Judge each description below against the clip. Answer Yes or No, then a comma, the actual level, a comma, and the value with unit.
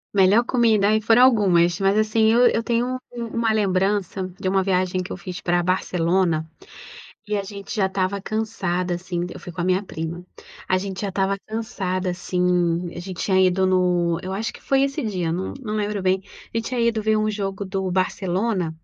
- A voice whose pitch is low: No, high, 190 Hz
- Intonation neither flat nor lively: Yes, average, 3.0 semitones